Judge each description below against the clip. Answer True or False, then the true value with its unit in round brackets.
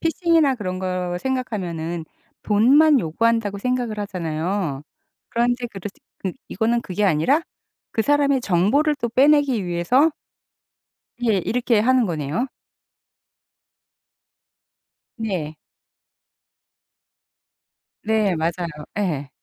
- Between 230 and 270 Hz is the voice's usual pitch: False (215 Hz)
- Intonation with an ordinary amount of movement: False (6.3 semitones)